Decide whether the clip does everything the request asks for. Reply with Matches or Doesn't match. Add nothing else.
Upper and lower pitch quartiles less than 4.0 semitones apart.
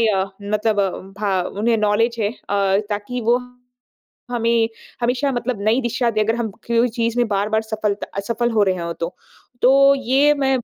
Matches